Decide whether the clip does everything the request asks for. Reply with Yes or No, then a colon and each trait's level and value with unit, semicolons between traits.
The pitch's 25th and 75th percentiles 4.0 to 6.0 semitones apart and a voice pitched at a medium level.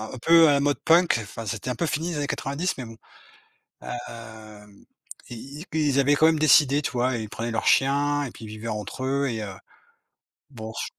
No: average, 4.4 semitones; low, 130 Hz